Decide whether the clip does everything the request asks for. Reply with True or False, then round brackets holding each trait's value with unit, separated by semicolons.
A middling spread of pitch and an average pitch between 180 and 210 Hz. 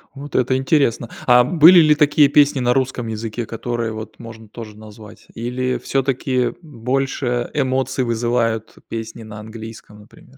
False (3.1 semitones; 120 Hz)